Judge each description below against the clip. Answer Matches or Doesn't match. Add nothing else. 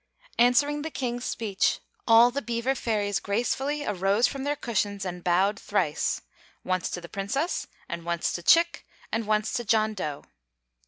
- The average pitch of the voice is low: Doesn't match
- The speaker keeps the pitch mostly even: Doesn't match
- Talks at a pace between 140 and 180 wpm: Matches